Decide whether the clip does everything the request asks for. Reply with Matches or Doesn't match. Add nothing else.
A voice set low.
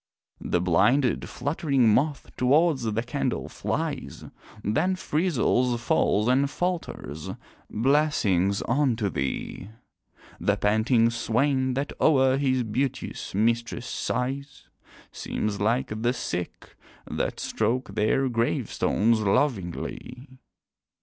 Matches